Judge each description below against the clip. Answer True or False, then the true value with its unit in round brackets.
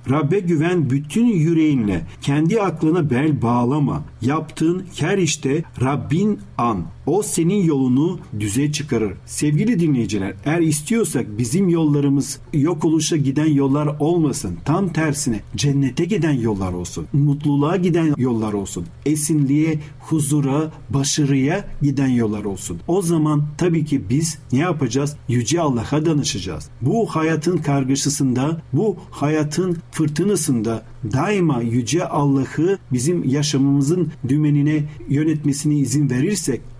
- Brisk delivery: False (115 wpm)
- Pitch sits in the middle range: True (145 Hz)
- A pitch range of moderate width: True (3.5 semitones)